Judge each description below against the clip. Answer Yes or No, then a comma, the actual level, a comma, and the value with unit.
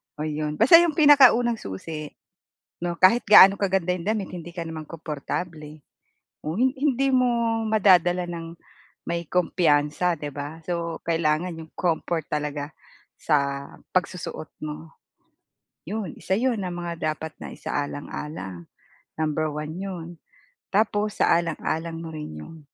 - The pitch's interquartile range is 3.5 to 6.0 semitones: Yes, average, 4.2 semitones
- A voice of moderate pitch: Yes, medium, 170 Hz